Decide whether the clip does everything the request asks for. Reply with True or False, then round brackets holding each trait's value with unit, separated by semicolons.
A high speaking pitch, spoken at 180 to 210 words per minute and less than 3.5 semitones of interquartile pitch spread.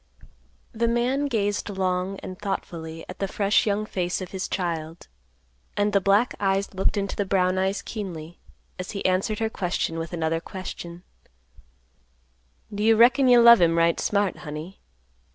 False (195 Hz; 160 wpm; 3.0 semitones)